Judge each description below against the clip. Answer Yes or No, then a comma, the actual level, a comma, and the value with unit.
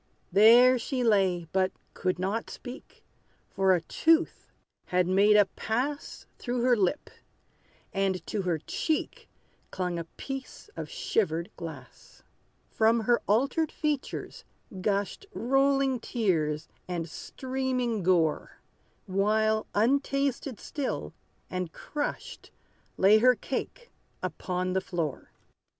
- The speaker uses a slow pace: Yes, slow, 110 wpm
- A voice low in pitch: No, high, 215 Hz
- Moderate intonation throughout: No, wide, 6.0 semitones